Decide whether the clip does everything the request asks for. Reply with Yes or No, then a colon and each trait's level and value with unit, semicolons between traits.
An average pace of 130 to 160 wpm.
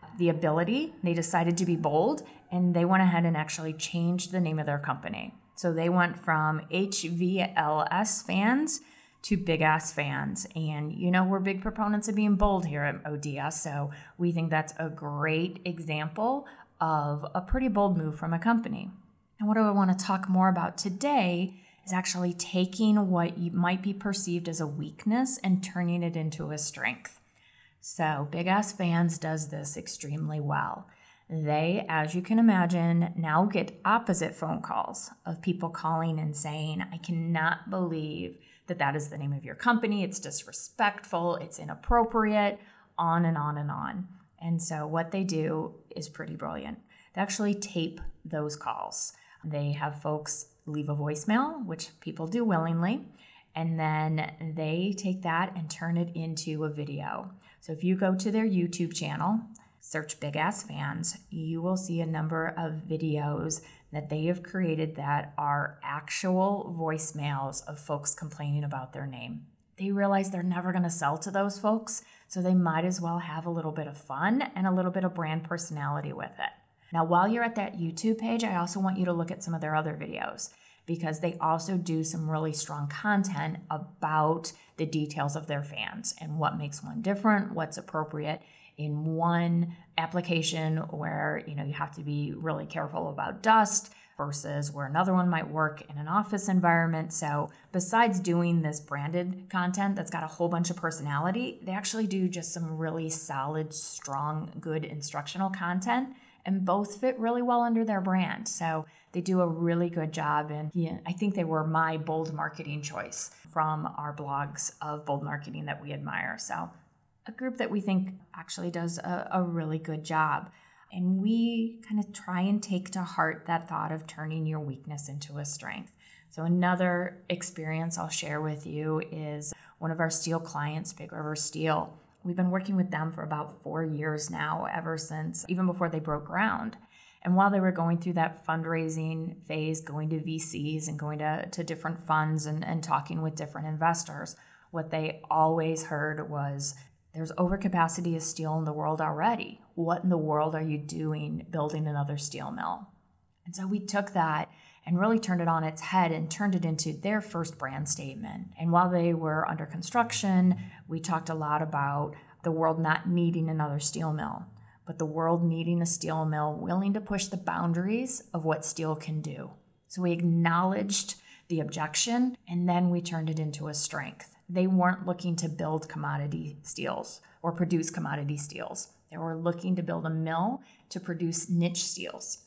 No: average, 180 wpm